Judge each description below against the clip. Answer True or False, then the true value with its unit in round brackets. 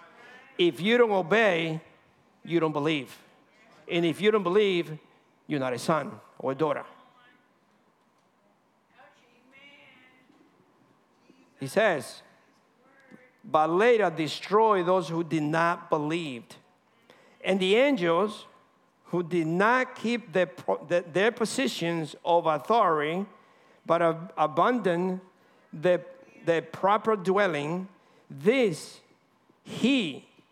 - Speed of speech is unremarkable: False (100 wpm)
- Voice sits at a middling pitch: True (180 Hz)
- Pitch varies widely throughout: False (4.7 semitones)